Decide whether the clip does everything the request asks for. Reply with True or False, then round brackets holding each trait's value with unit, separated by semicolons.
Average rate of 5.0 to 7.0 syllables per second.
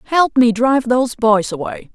True (5.3 syllables/s)